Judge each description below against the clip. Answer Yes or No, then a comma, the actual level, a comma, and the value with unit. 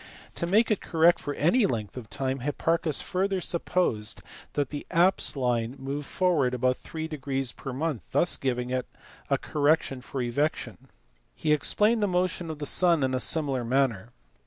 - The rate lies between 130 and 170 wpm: Yes, average, 160 wpm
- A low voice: No, medium, 145 Hz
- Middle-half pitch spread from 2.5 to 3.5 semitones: No, average, 4.9 semitones